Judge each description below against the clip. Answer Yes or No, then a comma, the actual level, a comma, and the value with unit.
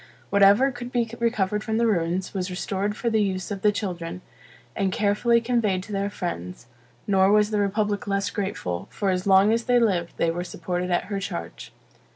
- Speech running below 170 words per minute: No, average, 195 wpm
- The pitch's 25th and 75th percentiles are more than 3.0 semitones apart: No, average, 2.7 semitones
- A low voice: No, high, 200 Hz